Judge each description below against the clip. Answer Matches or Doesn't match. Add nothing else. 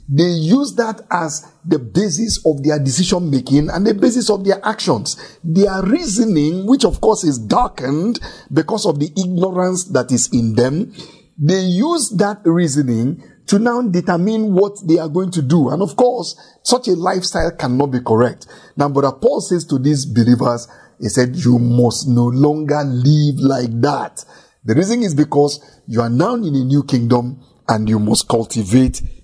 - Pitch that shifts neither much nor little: Doesn't match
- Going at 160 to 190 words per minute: Matches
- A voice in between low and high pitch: Matches